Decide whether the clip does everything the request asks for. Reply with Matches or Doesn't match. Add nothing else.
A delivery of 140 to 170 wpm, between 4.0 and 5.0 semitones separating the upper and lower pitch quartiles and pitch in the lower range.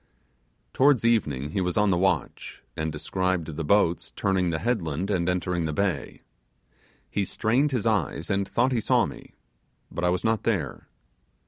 Matches